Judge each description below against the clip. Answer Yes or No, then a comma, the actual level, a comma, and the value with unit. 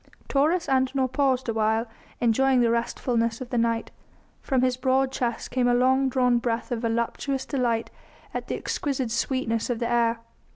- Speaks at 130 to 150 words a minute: No, average, 165 wpm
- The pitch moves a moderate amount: No, narrow, 2.2 semitones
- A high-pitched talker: Yes, high, 245 Hz